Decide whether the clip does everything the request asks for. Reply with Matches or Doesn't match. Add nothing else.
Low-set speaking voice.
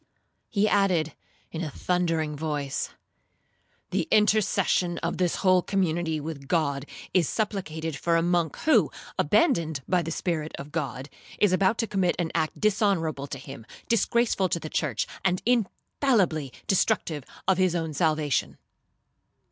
Doesn't match